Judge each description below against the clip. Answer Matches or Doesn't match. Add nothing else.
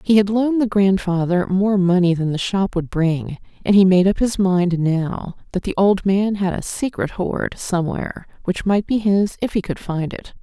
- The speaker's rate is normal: Doesn't match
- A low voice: Doesn't match